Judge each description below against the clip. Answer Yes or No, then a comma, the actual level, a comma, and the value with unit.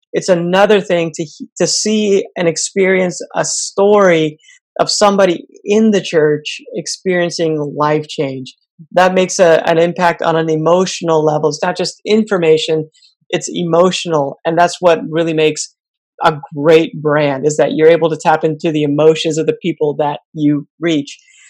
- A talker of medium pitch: Yes, medium, 165 Hz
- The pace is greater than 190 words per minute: No, average, 155 wpm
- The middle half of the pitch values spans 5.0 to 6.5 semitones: No, average, 2.9 semitones